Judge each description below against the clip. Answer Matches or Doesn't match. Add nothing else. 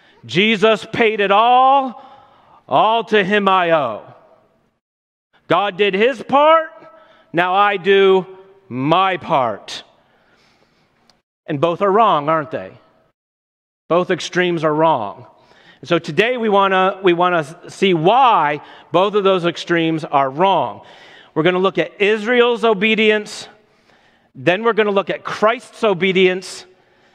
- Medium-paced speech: Doesn't match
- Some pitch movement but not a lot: Matches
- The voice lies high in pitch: Matches